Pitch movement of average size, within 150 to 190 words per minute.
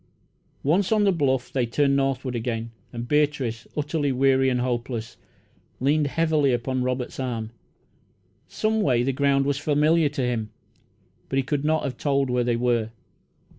Yes: average, 3.1 semitones; average, 160 wpm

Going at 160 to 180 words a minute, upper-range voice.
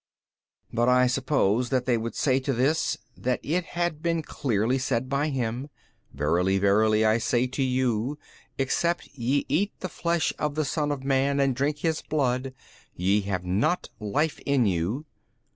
No: average, 170 wpm; low, 130 Hz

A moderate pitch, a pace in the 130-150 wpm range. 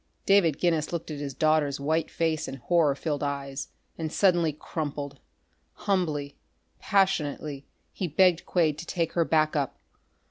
Yes: medium, 155 Hz; average, 145 wpm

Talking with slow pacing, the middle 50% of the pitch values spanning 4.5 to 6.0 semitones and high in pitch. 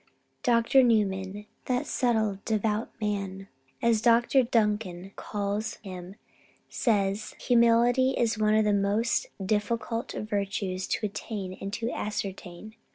No: slow, 130 wpm; average, 2.7 semitones; high, 215 Hz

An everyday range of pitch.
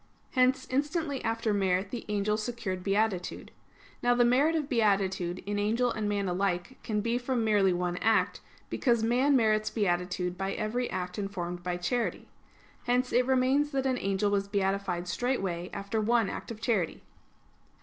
Yes: average, 4.2 semitones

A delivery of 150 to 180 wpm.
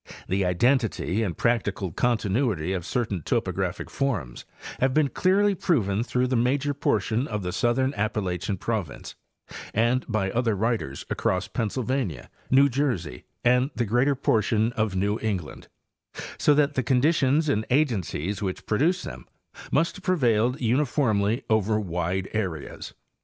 No: average, 140 wpm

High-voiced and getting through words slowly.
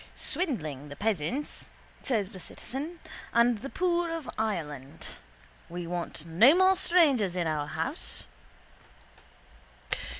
Yes: high, 220 Hz; slow, 110 wpm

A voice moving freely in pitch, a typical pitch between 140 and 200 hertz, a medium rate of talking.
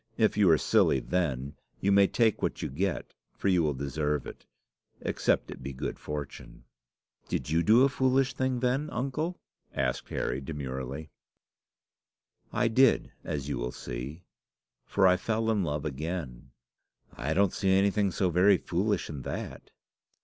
No: wide, 6.9 semitones; very low, 90 Hz; average, 155 wpm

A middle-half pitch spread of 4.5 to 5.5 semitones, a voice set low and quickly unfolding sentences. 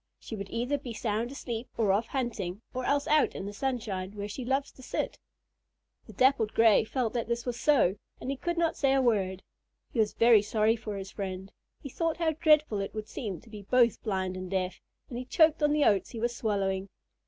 No: average, 4.8 semitones; high, 230 Hz; fast, 220 wpm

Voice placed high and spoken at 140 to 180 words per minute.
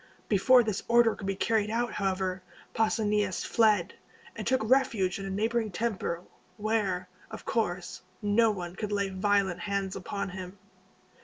Yes: high, 205 Hz; average, 150 wpm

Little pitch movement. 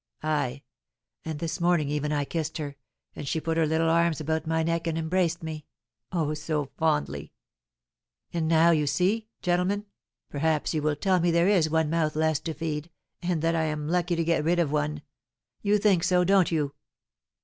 Yes: narrow, 2.0 semitones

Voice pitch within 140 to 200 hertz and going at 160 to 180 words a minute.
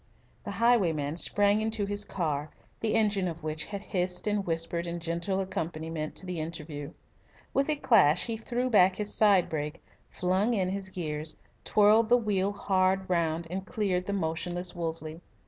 Yes: medium, 185 Hz; average, 165 wpm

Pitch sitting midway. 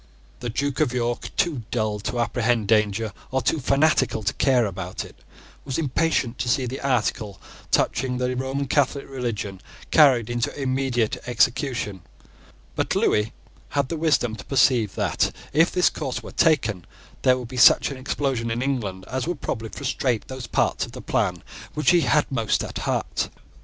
No: low, 125 Hz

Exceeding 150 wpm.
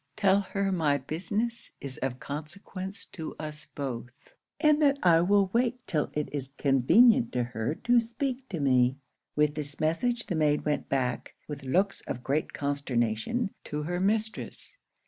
Yes: average, 160 wpm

